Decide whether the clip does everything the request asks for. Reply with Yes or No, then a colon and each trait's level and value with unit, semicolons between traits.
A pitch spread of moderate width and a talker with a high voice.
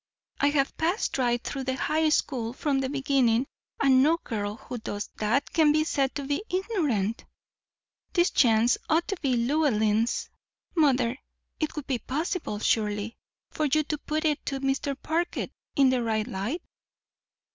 Yes: average, 4.7 semitones; very high, 270 Hz